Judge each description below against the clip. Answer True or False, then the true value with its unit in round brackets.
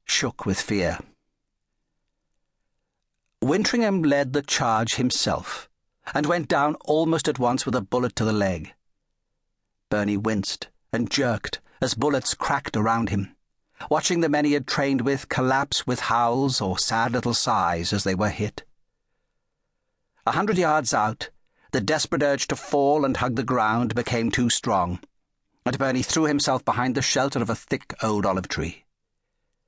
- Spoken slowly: False (155 wpm)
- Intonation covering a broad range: False (4.1 semitones)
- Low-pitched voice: True (130 Hz)